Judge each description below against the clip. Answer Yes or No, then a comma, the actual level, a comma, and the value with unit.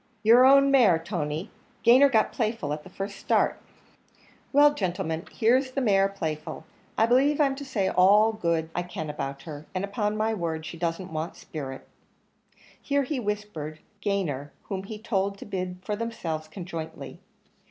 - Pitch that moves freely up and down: Yes, wide, 5.7 semitones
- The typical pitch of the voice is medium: No, high, 195 Hz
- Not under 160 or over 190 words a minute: Yes, average, 165 wpm